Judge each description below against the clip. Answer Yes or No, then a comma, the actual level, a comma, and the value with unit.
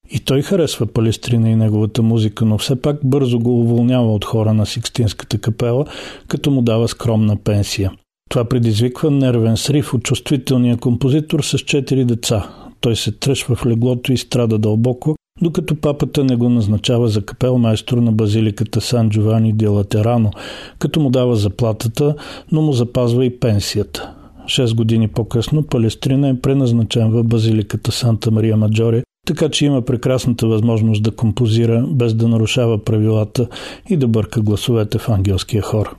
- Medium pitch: No, low, 120 Hz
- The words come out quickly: No, average, 155 wpm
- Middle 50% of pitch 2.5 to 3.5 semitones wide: Yes, average, 2.8 semitones